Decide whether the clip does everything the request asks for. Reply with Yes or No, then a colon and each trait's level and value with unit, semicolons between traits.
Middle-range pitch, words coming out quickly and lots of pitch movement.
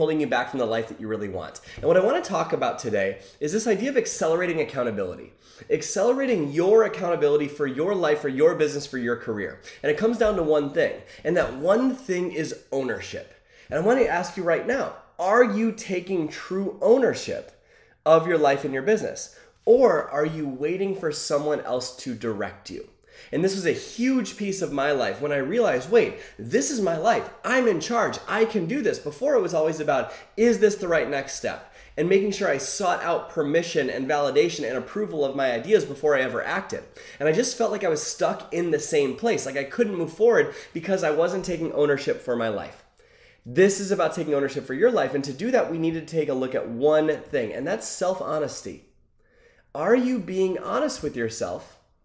Yes: medium, 180 Hz; fast, 215 wpm; wide, 8.3 semitones